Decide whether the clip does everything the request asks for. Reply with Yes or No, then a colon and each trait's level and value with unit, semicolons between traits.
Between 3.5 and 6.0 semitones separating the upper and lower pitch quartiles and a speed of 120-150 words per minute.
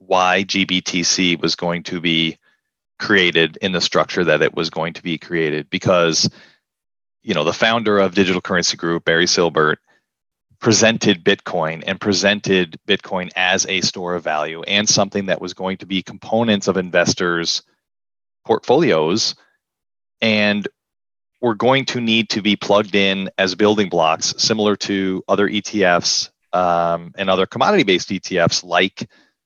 No: average, 2.9 semitones; average, 145 wpm